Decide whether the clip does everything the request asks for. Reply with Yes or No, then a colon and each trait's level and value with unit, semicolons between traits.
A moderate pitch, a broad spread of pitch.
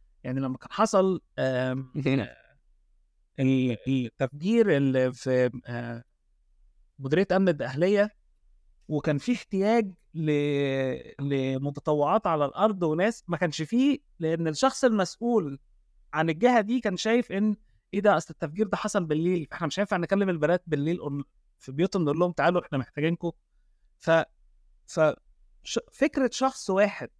Yes: medium, 160 Hz; wide, 6.9 semitones